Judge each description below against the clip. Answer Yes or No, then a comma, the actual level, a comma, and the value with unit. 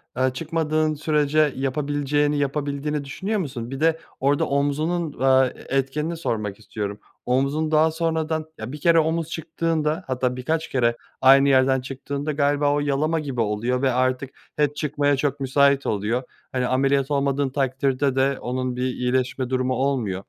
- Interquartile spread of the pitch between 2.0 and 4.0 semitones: Yes, average, 2.7 semitones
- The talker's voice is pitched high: No, medium, 140 Hz